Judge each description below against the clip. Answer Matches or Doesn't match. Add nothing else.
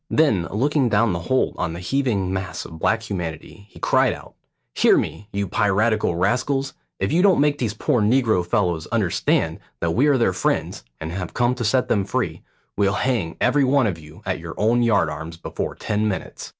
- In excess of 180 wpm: Matches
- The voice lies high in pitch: Doesn't match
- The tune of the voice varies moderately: Doesn't match